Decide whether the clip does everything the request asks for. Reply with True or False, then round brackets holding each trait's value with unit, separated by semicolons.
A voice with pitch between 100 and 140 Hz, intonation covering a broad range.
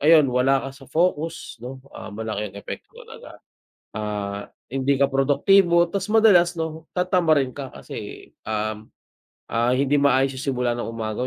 True (135 Hz; 5.8 semitones)